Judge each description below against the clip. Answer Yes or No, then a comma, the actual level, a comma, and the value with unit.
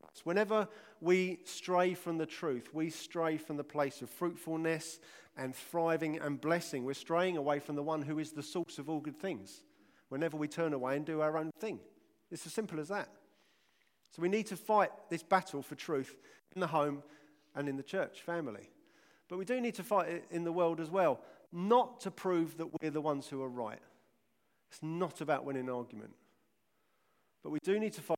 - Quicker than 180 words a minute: Yes, fast, 205 wpm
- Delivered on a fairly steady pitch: No, average, 3.4 semitones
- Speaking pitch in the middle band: Yes, medium, 165 Hz